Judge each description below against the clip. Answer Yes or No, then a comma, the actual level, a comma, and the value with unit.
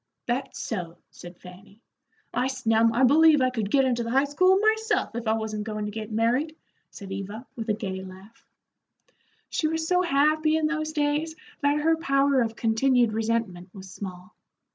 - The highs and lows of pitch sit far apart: Yes, wide, 5.8 semitones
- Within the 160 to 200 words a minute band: Yes, average, 180 wpm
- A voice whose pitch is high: Yes, high, 240 Hz